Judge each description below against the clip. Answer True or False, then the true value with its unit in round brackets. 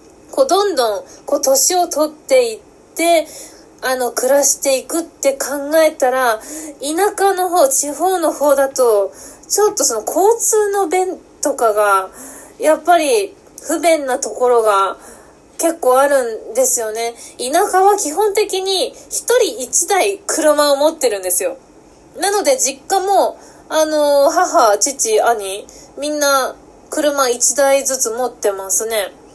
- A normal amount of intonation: False (6.3 semitones)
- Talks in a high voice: True (295 Hz)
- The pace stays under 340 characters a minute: True (245 characters per minute)